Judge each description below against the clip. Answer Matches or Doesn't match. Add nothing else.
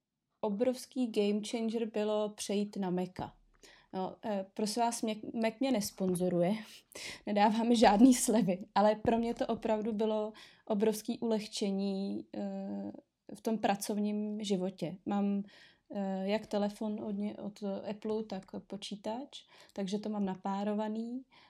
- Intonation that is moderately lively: Doesn't match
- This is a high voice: Matches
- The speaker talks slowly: Matches